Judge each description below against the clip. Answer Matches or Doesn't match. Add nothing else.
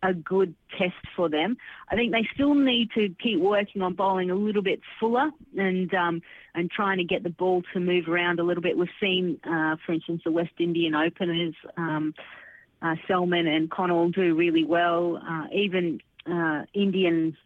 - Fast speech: Doesn't match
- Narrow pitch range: Matches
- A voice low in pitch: Doesn't match